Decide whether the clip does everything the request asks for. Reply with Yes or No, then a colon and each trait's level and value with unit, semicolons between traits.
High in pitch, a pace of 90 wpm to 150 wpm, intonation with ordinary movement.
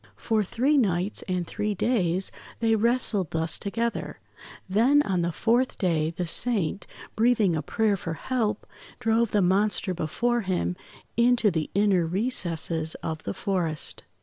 Yes: high, 200 Hz; average, 145 wpm; average, 5.0 semitones